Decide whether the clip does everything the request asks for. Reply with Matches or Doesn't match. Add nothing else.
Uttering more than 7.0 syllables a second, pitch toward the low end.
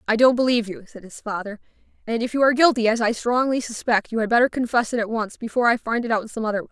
Doesn't match